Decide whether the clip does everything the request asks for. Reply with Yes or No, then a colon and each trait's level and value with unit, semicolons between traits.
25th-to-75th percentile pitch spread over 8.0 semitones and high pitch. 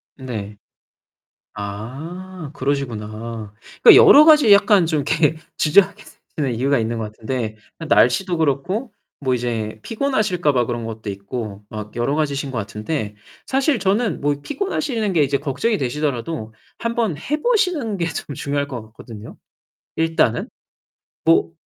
No: wide, 8.6 semitones; medium, 140 Hz